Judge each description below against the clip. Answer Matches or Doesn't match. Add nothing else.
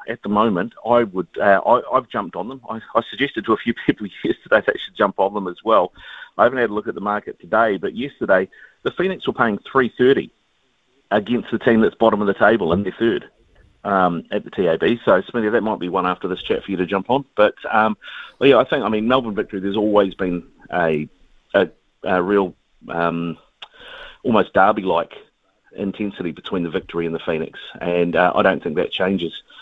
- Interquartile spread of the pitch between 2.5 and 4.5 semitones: Matches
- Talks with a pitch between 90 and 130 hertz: Matches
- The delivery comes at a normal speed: Doesn't match